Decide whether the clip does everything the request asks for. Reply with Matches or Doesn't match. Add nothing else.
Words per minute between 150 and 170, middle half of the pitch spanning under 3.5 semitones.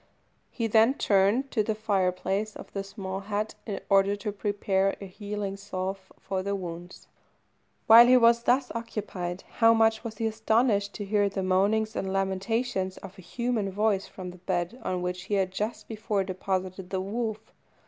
Doesn't match